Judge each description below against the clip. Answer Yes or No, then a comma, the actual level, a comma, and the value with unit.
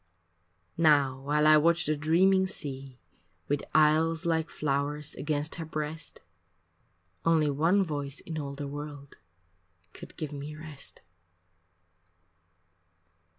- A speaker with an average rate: No, slow, 110 wpm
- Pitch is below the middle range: No, medium, 150 Hz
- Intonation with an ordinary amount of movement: No, narrow, 2.0 semitones